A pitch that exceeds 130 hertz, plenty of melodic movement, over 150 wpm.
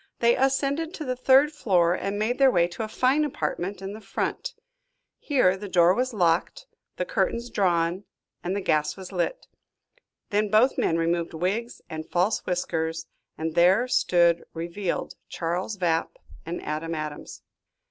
Yes: high, 190 Hz; wide, 6.1 semitones; average, 160 wpm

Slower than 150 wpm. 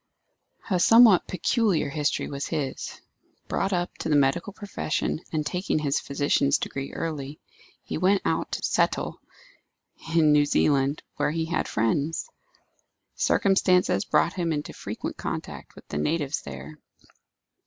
Yes: slow, 135 wpm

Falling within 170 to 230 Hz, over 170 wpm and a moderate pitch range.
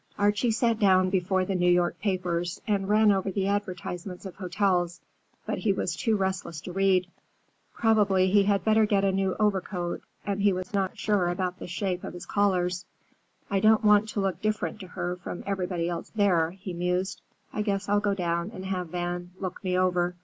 No: high, 190 Hz; average, 195 wpm; narrow, 2.3 semitones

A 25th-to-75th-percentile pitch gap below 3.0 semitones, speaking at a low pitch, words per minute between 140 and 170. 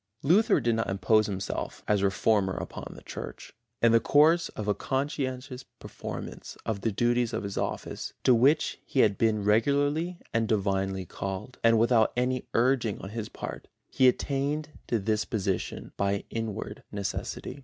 No: average, 4.5 semitones; low, 115 Hz; average, 160 wpm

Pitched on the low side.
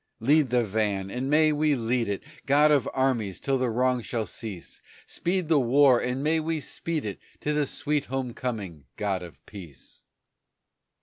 Yes: low, 125 Hz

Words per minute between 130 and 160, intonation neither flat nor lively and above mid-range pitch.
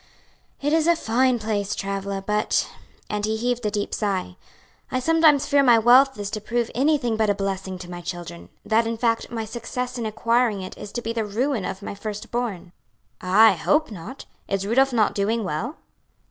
No: average, 200 wpm; average, 3.6 semitones; high, 220 Hz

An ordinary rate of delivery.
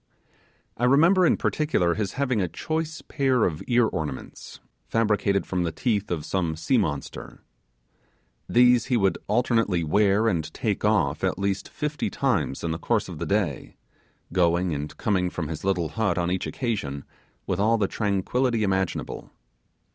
Yes: average, 160 wpm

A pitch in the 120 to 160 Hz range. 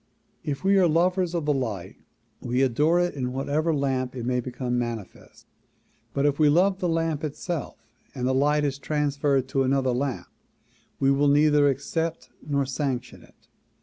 Yes: medium, 140 Hz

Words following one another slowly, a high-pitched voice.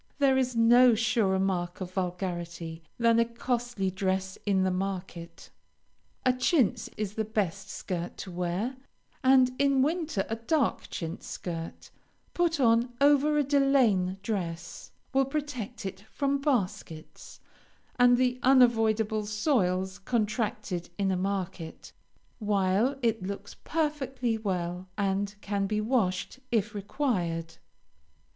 Yes: slow, 125 wpm; high, 215 Hz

